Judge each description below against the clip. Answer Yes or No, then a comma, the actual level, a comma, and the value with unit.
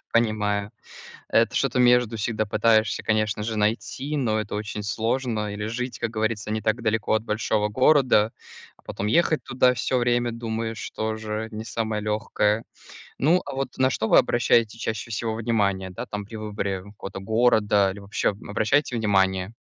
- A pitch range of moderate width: No, narrow, 1.9 semitones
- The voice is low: Yes, low, 110 Hz